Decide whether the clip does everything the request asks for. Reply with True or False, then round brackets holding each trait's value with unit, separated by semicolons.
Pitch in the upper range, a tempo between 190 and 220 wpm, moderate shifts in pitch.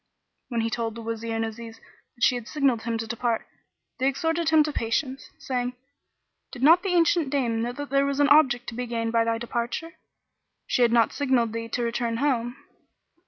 True (240 Hz; 205 wpm; 3.3 semitones)